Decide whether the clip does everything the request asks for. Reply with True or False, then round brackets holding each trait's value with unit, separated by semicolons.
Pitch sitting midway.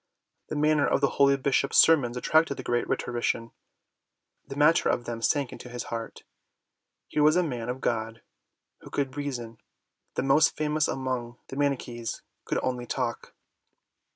False (130 Hz)